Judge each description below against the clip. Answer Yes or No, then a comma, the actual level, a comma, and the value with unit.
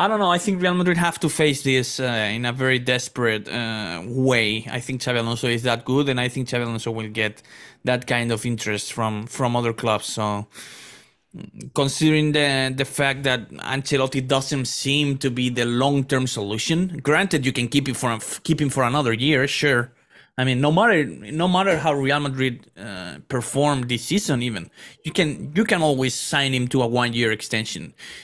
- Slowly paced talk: No, average, 200 wpm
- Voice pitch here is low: Yes, low, 130 Hz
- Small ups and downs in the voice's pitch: No, average, 3.4 semitones